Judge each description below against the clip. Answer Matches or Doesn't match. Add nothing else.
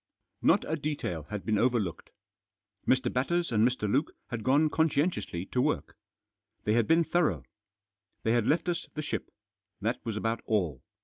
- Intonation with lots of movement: Matches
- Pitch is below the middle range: Matches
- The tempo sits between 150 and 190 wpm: Matches